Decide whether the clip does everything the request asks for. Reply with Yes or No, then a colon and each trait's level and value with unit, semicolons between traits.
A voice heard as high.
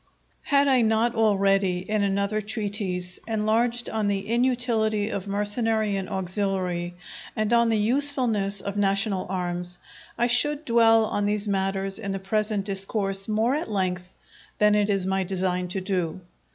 Yes: high, 205 Hz